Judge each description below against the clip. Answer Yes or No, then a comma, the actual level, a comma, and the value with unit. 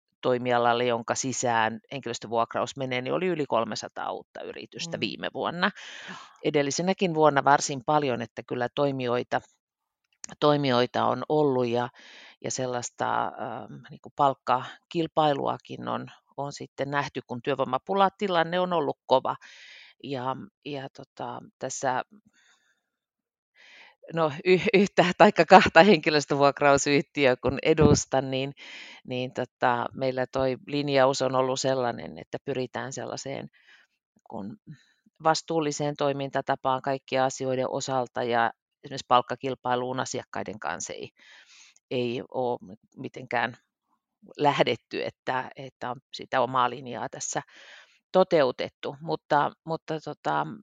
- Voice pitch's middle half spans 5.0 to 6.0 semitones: No, average, 3.2 semitones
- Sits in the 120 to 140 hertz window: Yes, low, 135 Hz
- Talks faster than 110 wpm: No, average, 105 wpm